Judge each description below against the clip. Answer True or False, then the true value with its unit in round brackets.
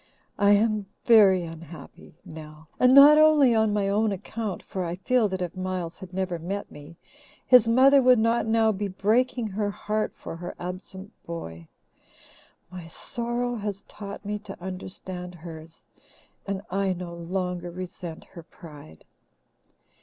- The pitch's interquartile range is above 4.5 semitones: False (3.9 semitones)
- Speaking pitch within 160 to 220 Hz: True (190 Hz)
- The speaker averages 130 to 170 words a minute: True (150 wpm)